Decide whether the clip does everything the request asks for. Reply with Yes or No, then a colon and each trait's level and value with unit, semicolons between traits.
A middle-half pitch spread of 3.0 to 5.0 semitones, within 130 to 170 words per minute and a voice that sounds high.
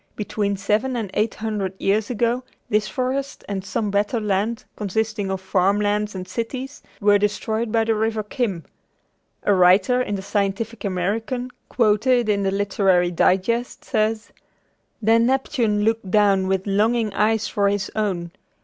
No: narrow, 2.4 semitones; average, 150 wpm; high, 210 Hz